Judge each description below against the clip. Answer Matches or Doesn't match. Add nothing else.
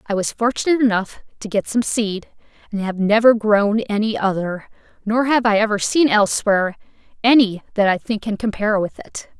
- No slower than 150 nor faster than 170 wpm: Doesn't match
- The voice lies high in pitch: Matches